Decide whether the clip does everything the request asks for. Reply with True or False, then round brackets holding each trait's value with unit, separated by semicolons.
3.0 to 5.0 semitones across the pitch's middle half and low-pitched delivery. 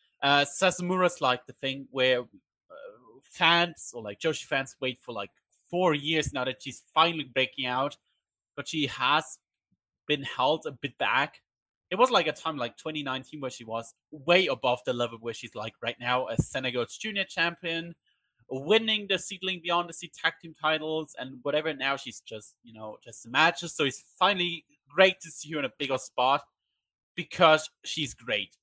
False (4.7 semitones; 145 Hz)